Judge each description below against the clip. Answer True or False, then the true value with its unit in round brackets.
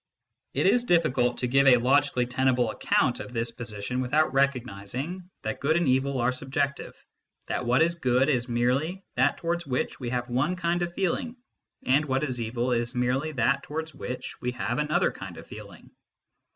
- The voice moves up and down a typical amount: True (3.7 semitones)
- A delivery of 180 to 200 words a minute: True (185 wpm)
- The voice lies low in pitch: True (130 Hz)